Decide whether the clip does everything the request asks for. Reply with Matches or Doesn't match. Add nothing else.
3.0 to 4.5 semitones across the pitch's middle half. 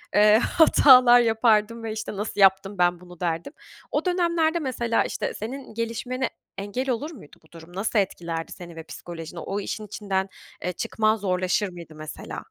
Doesn't match